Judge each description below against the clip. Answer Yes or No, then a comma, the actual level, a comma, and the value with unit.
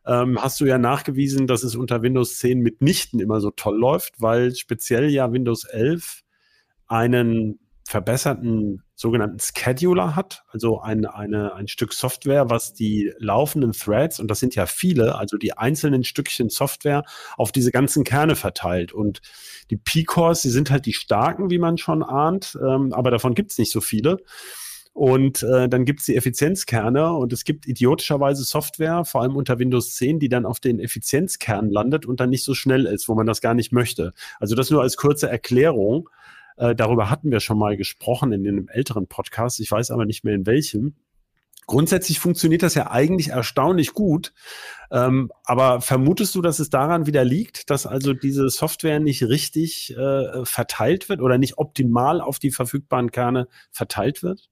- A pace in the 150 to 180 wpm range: Yes, average, 175 wpm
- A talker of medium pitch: No, low, 130 Hz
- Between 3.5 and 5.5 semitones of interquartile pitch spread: Yes, average, 4.1 semitones